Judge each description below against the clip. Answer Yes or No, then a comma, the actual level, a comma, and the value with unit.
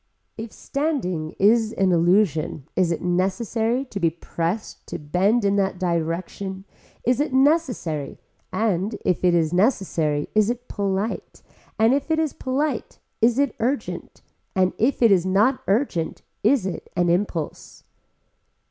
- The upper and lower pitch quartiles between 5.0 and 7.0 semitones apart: Yes, average, 5.3 semitones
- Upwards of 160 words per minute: No, average, 145 wpm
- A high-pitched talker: Yes, high, 200 Hz